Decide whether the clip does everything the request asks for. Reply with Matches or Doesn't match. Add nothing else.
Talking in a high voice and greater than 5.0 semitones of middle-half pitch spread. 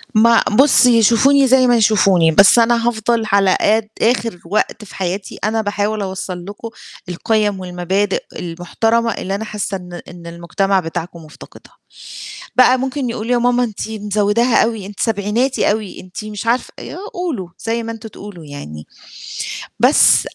Doesn't match